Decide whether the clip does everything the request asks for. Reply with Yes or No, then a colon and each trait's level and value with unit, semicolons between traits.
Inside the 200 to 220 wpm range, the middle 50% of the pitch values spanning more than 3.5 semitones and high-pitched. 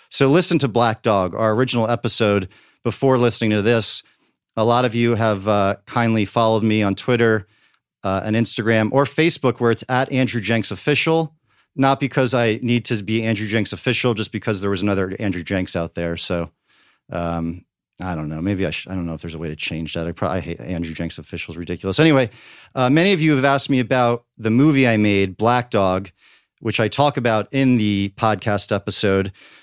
No: fast, 205 wpm; average, 4.0 semitones; low, 110 Hz